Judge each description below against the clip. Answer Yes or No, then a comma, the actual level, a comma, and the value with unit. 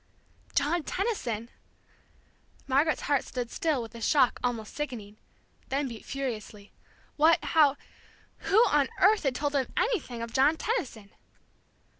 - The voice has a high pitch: Yes, very high, 275 Hz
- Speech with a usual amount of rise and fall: Yes, average, 4.8 semitones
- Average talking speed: No, slow, 130 wpm